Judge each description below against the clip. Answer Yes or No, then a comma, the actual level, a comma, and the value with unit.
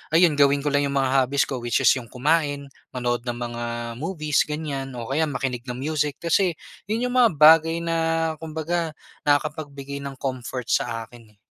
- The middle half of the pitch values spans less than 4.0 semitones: Yes, average, 3.6 semitones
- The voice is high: No, medium, 140 Hz